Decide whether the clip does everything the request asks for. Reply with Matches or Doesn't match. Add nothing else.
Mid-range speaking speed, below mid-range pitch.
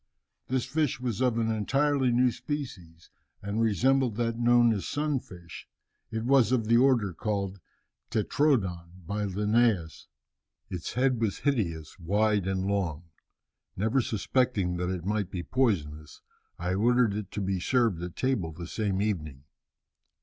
Matches